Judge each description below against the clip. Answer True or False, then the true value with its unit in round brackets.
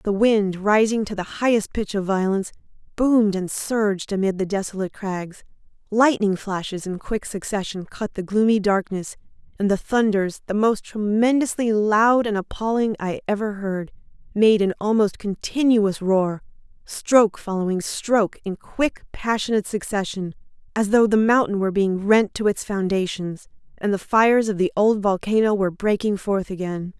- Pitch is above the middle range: True (205 Hz)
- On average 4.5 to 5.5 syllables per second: True (4.9 syllables/s)